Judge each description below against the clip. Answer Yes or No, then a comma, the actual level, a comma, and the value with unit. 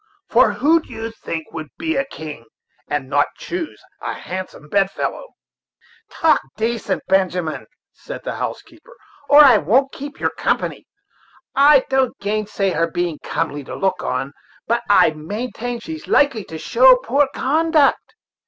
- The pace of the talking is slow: No, average, 155 wpm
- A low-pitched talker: No, high, 225 Hz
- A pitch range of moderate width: No, wide, 8.7 semitones